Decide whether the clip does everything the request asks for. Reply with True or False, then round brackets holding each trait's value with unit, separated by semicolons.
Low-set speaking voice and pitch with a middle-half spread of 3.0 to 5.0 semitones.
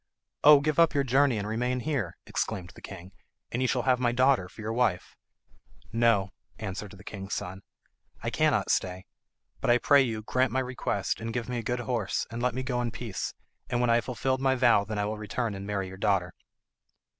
True (115 Hz; 3.8 semitones)